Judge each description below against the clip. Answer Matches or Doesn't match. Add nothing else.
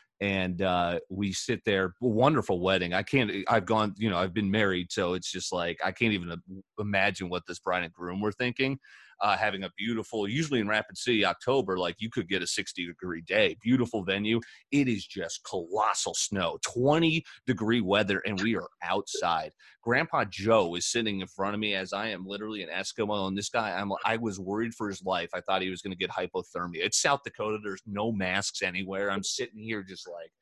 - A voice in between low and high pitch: Doesn't match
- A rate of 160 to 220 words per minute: Matches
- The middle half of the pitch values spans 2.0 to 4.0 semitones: Matches